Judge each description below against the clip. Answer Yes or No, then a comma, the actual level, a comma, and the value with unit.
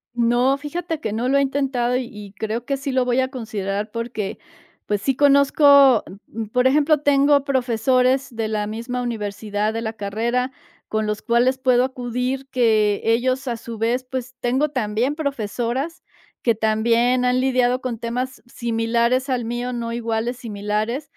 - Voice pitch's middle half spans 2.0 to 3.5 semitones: Yes, narrow, 2.6 semitones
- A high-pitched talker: Yes, high, 245 Hz